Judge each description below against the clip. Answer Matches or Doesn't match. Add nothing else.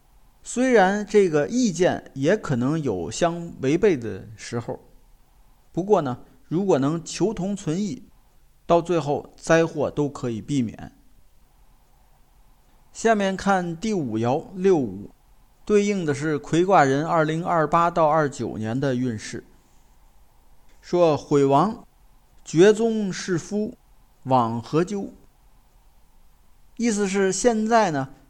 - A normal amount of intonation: Doesn't match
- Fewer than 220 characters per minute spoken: Matches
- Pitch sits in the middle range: Matches